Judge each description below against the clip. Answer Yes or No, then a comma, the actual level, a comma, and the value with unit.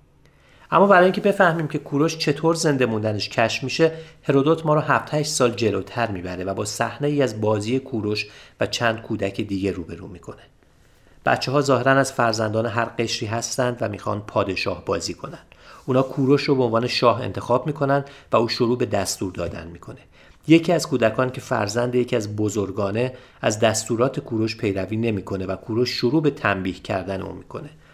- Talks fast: Yes, fast, 170 wpm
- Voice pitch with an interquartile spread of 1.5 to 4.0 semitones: No, average, 4.7 semitones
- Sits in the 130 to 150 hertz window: No, low, 115 Hz